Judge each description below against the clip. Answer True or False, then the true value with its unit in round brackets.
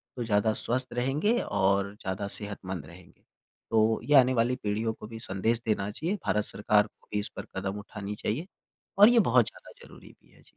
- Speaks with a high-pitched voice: False (105 Hz)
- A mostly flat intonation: False (3.3 semitones)